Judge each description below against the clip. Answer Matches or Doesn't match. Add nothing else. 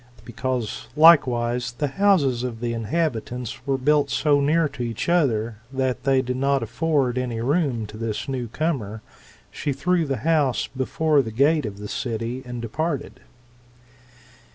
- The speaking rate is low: Doesn't match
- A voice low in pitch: Matches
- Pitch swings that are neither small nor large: Matches